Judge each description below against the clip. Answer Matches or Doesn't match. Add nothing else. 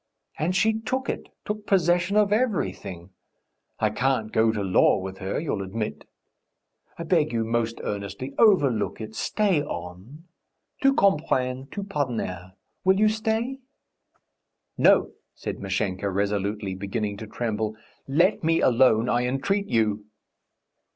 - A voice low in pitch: Matches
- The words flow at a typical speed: Doesn't match